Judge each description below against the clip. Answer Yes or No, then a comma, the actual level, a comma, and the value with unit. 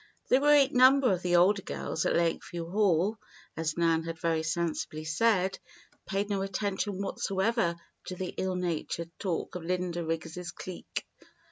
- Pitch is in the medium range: Yes, medium, 180 Hz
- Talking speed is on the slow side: No, average, 150 wpm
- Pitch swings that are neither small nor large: Yes, average, 3.1 semitones